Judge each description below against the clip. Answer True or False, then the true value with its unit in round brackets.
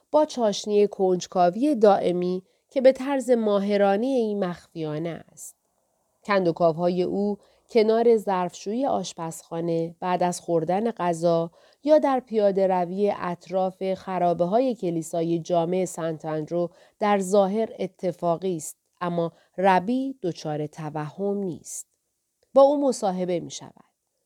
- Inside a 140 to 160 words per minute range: False (115 wpm)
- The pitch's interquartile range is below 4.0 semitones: True (3.5 semitones)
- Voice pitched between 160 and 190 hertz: True (185 Hz)